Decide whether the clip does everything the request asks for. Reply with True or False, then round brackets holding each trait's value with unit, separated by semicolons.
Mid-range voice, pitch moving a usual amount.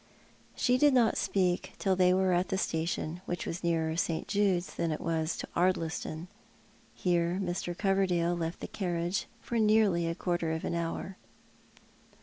False (175 Hz; 2.2 semitones)